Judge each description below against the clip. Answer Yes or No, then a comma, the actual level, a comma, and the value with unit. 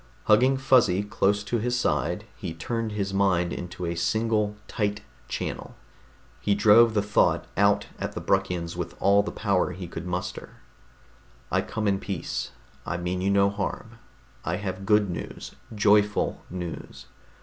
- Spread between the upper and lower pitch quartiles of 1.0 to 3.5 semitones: Yes, narrow, 2.6 semitones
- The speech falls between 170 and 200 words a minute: No, average, 155 wpm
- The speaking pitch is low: Yes, low, 100 Hz